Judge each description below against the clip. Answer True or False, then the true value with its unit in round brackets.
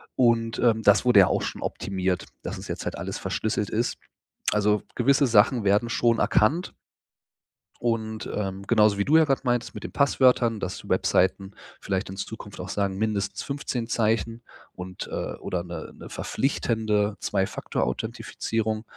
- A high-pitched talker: False (110 Hz)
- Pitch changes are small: False (3.0 semitones)